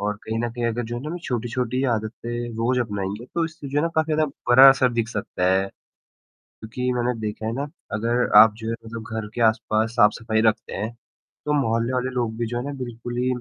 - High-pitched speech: No, low, 120 Hz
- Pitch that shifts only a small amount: Yes, narrow, 2.3 semitones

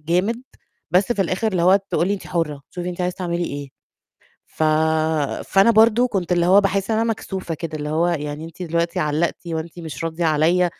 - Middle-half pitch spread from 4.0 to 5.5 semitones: No, average, 3.1 semitones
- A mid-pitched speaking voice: Yes, medium, 175 Hz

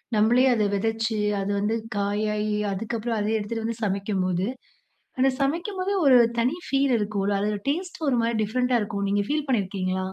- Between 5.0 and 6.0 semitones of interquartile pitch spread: No, average, 3.7 semitones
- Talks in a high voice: Yes, high, 220 Hz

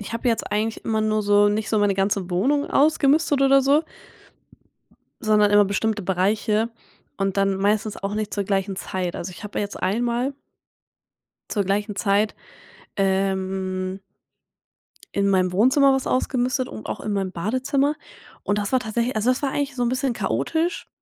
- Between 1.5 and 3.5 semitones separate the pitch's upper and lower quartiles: No, average, 4.3 semitones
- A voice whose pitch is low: No, high, 210 Hz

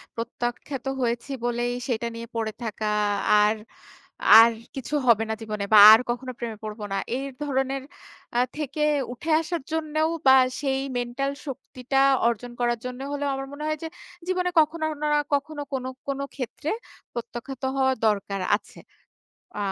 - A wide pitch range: No, average, 3.5 semitones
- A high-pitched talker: Yes, very high, 260 Hz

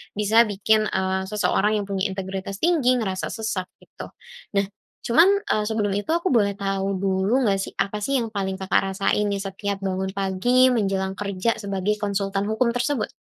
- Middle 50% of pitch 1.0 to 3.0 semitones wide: Yes, narrow, 2.6 semitones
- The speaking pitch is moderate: No, high, 200 Hz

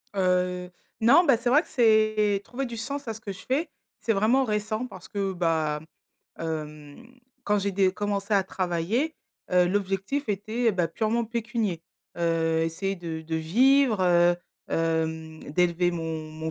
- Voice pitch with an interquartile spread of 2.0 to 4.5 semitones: No, average, 5.2 semitones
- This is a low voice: No, high, 195 Hz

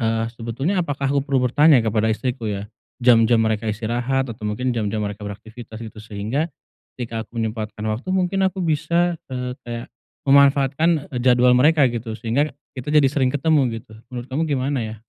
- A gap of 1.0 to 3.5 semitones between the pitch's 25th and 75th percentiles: No, average, 4.2 semitones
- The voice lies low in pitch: Yes, low, 125 Hz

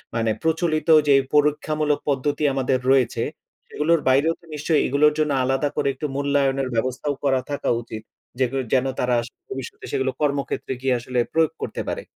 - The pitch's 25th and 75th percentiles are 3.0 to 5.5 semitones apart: No, narrow, 2.4 semitones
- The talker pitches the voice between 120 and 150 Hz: Yes, medium, 140 Hz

